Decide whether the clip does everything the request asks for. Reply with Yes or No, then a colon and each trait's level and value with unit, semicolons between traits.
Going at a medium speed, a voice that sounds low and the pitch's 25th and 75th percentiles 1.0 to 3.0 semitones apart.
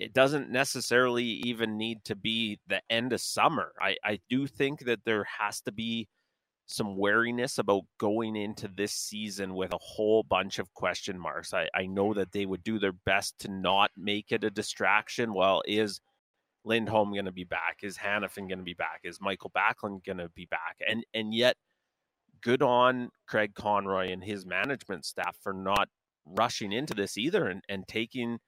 Yes: average, 180 wpm; low, 105 Hz; average, 2.7 semitones